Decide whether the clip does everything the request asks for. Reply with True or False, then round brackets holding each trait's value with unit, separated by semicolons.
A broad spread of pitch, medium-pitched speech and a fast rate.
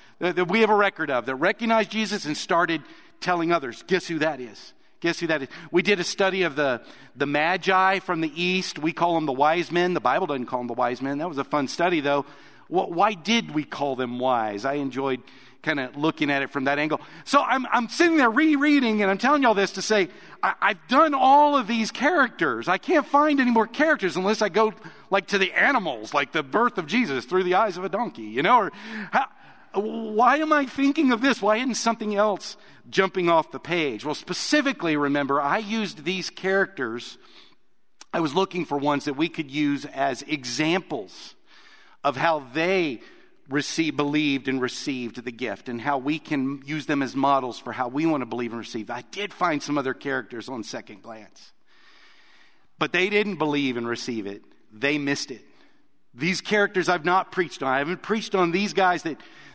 True (6.9 semitones; 170 Hz; 210 wpm)